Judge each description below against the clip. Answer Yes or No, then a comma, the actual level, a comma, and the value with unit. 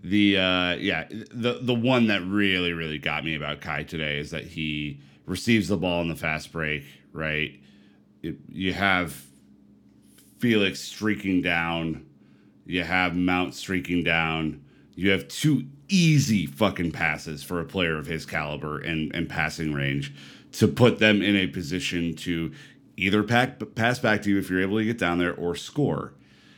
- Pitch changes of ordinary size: Yes, average, 4.7 semitones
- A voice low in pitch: Yes, very low, 85 Hz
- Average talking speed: Yes, average, 165 wpm